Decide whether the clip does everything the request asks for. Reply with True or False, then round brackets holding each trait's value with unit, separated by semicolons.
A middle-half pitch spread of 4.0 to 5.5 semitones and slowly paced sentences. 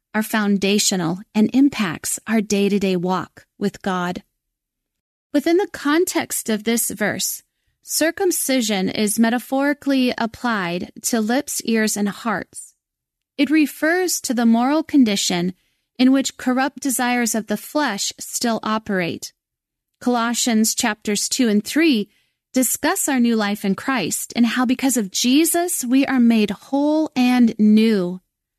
True (4.6 semitones; 130 wpm)